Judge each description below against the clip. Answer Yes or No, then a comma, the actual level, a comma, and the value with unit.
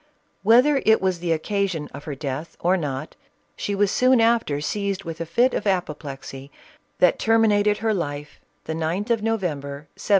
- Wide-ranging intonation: Yes, wide, 6.0 semitones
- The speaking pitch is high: No, medium, 180 Hz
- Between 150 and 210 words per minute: Yes, average, 170 wpm